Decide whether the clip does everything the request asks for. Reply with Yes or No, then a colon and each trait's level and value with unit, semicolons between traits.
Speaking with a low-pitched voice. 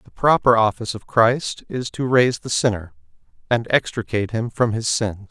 Yes: low, 115 Hz